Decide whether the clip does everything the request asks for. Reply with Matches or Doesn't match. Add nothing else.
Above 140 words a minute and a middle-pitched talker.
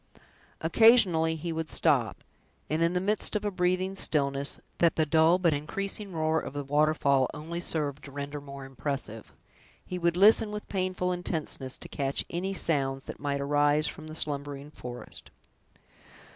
Matches